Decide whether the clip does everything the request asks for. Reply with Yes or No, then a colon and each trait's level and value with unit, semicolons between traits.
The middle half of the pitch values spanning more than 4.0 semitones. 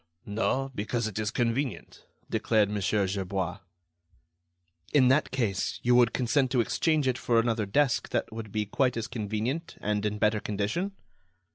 No: average, 3.6 semitones